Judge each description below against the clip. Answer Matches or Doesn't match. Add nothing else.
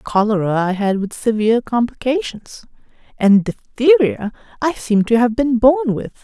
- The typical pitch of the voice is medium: Doesn't match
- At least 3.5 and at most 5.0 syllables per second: Matches